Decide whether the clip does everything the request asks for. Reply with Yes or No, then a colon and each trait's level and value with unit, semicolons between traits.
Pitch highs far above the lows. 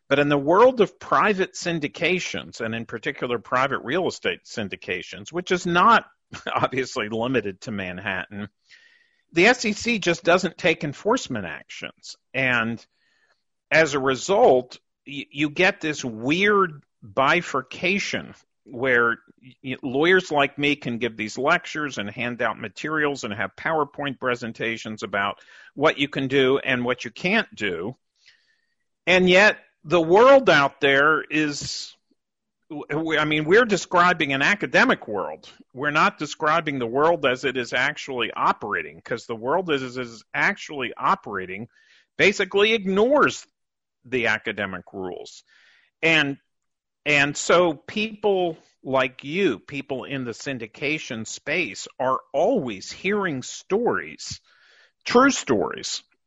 Yes: wide, 6.5 semitones